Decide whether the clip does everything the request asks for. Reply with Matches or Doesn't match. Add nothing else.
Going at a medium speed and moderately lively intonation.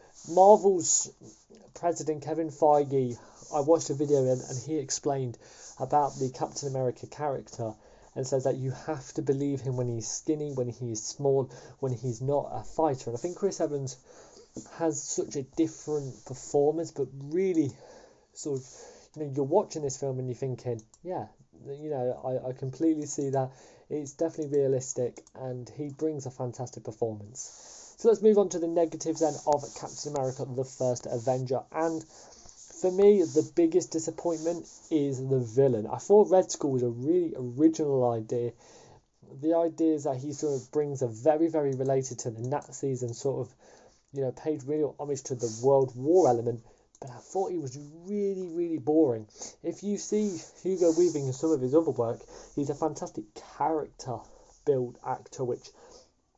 Matches